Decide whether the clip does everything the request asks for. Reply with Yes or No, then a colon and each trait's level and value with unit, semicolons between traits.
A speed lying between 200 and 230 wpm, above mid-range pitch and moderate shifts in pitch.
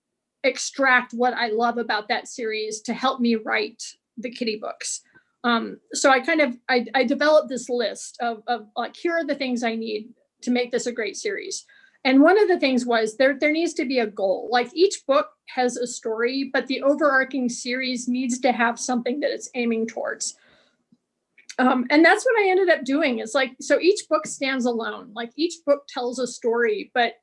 Yes: fast, 205 wpm; very high, 255 Hz; average, 3.4 semitones